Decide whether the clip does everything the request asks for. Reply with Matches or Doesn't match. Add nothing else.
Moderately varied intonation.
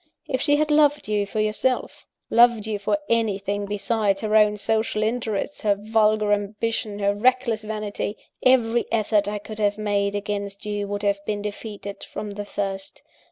Doesn't match